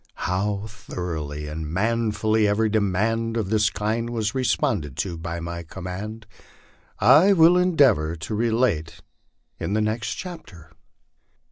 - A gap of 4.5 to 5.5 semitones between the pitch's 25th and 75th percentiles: Yes, average, 5.0 semitones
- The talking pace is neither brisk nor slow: No, slow, 130 wpm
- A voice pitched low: Yes, low, 105 Hz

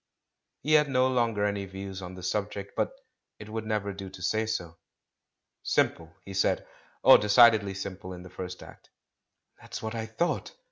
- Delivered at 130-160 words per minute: No, average, 175 wpm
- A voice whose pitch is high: No, low, 100 Hz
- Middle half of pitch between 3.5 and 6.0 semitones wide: No, average, 2.9 semitones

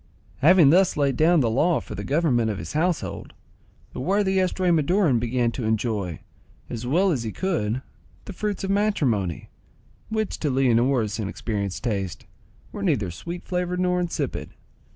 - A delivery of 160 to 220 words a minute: No, average, 150 wpm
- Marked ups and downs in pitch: Yes, wide, 8.1 semitones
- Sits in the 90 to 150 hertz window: Yes, medium, 140 Hz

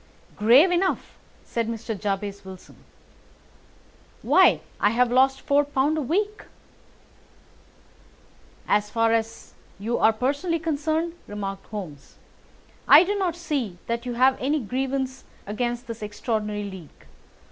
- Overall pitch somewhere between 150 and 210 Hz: No, high, 240 Hz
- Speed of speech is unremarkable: No, slow, 125 wpm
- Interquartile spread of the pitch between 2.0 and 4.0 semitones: No, wide, 5.4 semitones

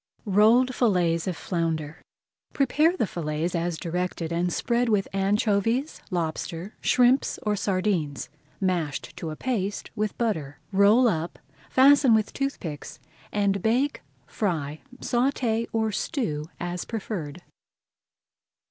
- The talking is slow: Yes, slow, 115 wpm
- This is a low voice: No, high, 195 Hz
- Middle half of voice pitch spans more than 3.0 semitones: Yes, wide, 5.5 semitones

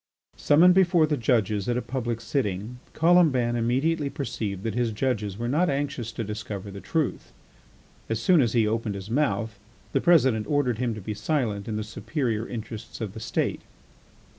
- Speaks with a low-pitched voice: Yes, low, 120 Hz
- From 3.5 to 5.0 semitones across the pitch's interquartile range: Yes, average, 4.7 semitones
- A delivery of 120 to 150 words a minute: No, average, 175 wpm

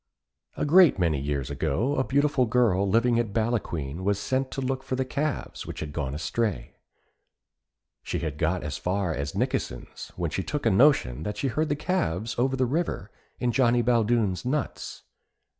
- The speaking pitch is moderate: No, low, 115 Hz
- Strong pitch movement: Yes, wide, 7.4 semitones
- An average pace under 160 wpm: No, average, 175 wpm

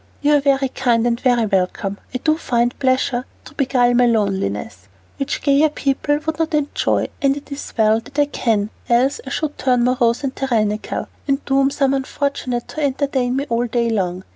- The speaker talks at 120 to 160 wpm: No, average, 190 wpm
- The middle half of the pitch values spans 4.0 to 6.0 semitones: No, average, 3.2 semitones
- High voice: Yes, very high, 255 Hz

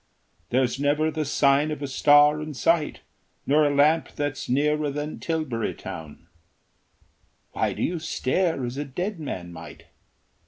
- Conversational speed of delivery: Yes, average, 150 wpm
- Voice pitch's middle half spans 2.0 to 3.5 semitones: Yes, narrow, 2.6 semitones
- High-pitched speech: No, medium, 145 Hz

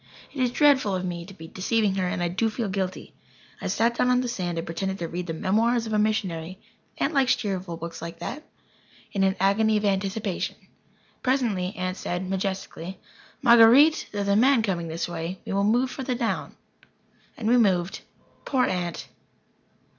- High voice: Yes, high, 195 Hz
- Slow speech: No, average, 185 wpm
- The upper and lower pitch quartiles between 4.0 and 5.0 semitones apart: Yes, average, 4.4 semitones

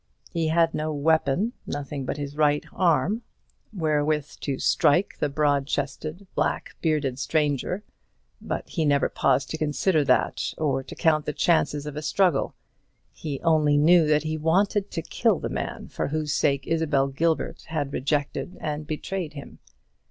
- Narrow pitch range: Yes, narrow, 2.2 semitones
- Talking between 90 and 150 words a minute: No, average, 160 wpm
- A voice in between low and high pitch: Yes, medium, 150 Hz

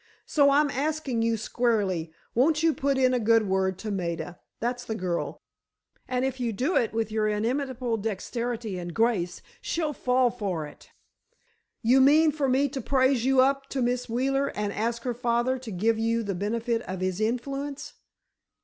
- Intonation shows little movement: No, average, 3.8 semitones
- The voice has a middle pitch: No, high, 235 Hz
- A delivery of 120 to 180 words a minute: Yes, average, 165 wpm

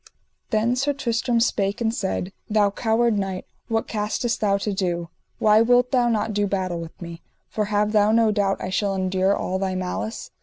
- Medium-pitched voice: No, high, 210 Hz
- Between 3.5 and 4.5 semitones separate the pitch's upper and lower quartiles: No, average, 3.0 semitones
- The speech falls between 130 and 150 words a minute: No, average, 190 wpm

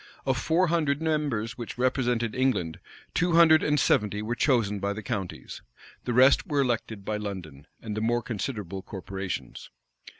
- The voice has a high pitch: No, low, 115 Hz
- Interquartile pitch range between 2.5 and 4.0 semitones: No, average, 5.0 semitones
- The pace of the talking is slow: No, average, 160 wpm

